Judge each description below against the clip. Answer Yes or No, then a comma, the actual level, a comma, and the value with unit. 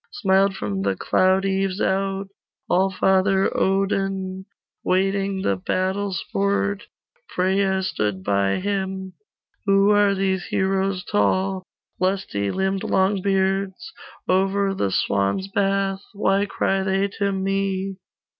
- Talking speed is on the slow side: Yes, slow, 110 wpm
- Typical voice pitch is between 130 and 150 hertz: No, high, 195 Hz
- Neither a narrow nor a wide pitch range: No, narrow, 0.7 semitones